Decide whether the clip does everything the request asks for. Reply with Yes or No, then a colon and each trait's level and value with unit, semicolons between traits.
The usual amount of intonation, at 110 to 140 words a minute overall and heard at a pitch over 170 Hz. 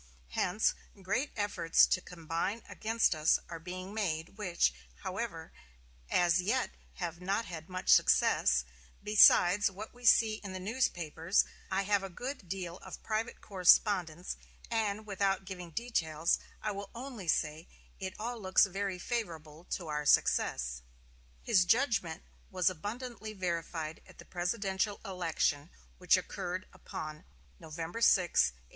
Yes: average, 4.0 semitones; slow, 135 wpm; medium, 185 Hz